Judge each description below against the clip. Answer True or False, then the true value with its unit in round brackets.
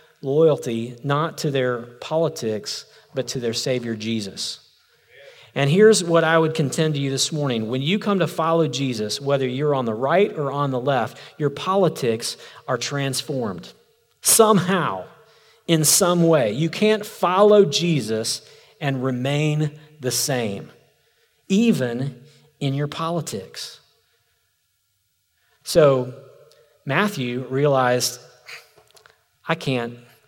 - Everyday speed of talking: False (120 wpm)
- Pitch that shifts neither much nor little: True (4.7 semitones)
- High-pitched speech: False (140 Hz)